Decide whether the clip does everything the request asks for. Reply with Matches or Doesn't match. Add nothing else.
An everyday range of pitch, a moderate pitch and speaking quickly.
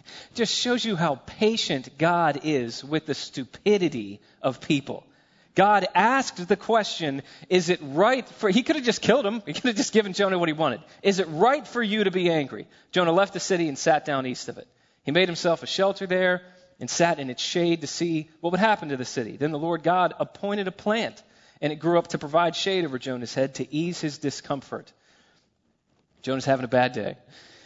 Doesn't match